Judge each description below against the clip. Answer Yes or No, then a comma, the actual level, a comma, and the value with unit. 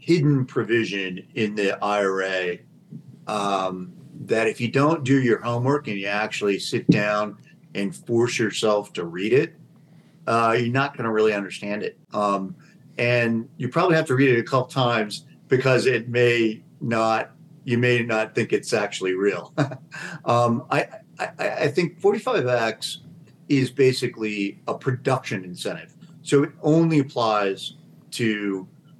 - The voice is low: Yes, low, 120 Hz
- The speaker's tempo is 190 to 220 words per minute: No, average, 145 wpm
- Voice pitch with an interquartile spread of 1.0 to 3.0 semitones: No, average, 4.9 semitones